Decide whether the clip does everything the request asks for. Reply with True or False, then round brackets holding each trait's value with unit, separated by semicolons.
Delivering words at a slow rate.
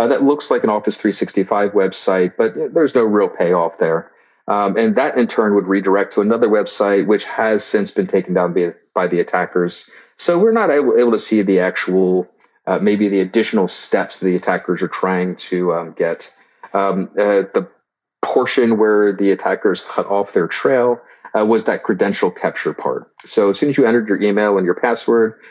False (195 wpm)